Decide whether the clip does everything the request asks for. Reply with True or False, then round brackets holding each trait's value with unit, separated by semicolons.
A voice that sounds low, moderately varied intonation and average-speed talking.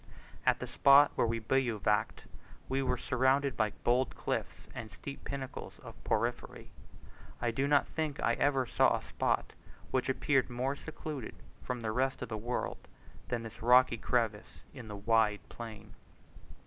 True (125 Hz; 3.0 semitones; 160 wpm)